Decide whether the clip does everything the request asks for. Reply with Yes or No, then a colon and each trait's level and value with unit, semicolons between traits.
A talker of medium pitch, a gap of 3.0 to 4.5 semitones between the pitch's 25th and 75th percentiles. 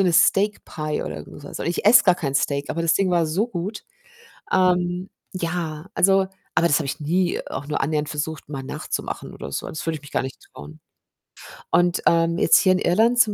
Yes: medium, 170 Hz; average, 3.6 semitones